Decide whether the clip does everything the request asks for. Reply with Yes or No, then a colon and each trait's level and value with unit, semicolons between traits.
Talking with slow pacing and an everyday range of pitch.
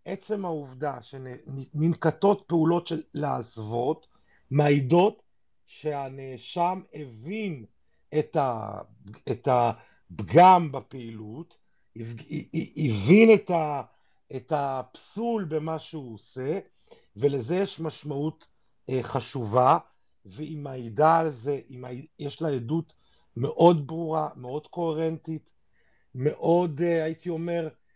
Yes: slow, 75 wpm; average, 4.1 semitones